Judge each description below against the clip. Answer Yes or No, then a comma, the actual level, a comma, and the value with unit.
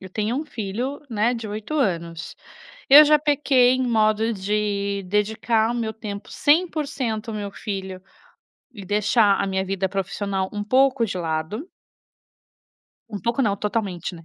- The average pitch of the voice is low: No, high, 210 Hz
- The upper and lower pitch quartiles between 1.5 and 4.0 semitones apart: Yes, average, 3.7 semitones